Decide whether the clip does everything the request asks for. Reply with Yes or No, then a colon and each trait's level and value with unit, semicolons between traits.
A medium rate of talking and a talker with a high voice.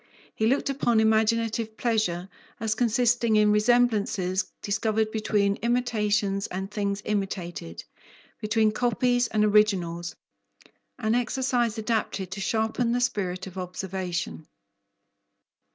No: slow, 105 wpm; high, 215 Hz